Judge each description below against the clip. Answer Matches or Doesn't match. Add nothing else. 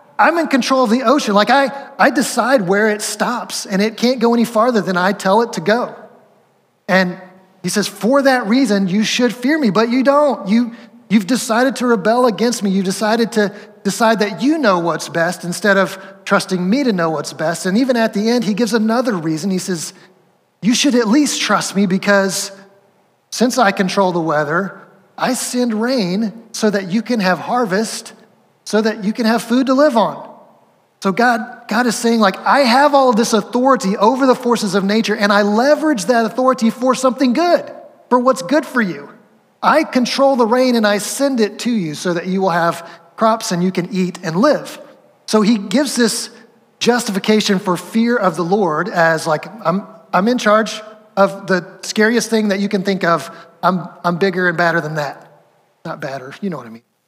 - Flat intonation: Doesn't match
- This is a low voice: Doesn't match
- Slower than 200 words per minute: Doesn't match